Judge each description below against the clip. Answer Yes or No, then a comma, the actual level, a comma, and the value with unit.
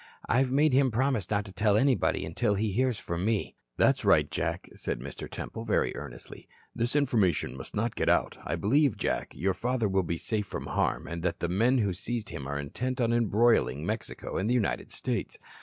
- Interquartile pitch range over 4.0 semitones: Yes, average, 4.9 semitones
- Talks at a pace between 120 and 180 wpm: No, fast, 205 wpm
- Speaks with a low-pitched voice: Yes, low, 110 Hz